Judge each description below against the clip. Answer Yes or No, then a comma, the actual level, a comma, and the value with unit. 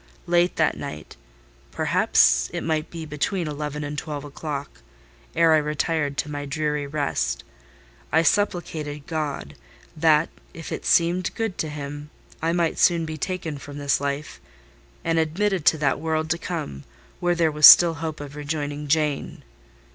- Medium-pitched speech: Yes, medium, 150 Hz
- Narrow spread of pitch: Yes, narrow, 2.3 semitones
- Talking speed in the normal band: Yes, average, 150 wpm